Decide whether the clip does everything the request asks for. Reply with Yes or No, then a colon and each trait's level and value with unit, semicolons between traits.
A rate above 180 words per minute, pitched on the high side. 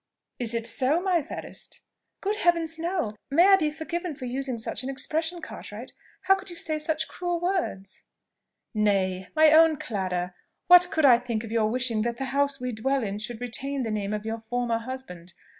Yes: average, 190 wpm; very high, 260 Hz